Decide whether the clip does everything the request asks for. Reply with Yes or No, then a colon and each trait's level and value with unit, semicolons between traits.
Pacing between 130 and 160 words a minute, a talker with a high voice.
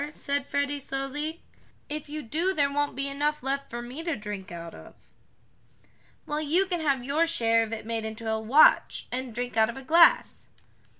No: average, 190 wpm; very high, 275 Hz